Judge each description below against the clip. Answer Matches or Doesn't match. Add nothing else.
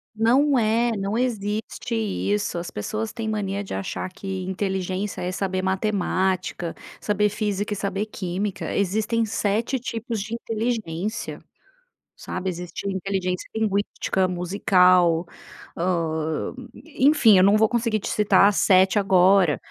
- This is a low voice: Doesn't match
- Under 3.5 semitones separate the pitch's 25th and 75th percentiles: Matches